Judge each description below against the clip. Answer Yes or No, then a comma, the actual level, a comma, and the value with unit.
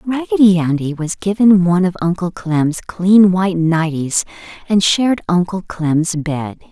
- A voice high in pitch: No, medium, 180 Hz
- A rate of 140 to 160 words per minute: Yes, average, 145 wpm